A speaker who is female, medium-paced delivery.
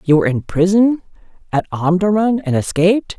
Yes: female; average, 150 wpm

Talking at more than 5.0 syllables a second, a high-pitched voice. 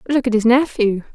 Yes: 5.8 syllables/s; high, 235 Hz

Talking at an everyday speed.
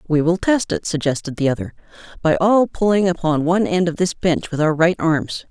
No: fast, 220 wpm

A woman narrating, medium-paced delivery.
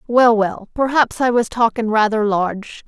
Yes: female; average, 165 wpm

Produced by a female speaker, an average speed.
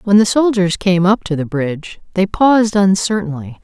Yes: female; average, 180 wpm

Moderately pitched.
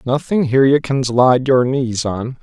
No: low, 130 Hz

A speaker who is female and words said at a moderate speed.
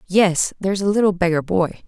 Yes: female; average, 190 wpm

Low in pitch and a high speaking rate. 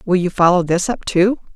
No: medium, 185 Hz; fast, 230 wpm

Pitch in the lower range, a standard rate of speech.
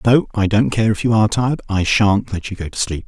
No: low, 105 Hz; fast, 290 wpm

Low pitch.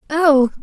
No: very high, 290 Hz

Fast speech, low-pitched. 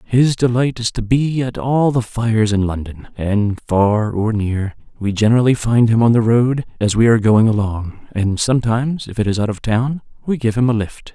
Yes: fast, 215 wpm; low, 115 Hz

